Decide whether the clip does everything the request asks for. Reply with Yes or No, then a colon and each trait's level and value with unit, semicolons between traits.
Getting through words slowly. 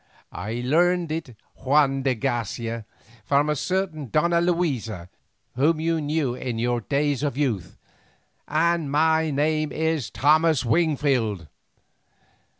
Yes: slow, 120 wpm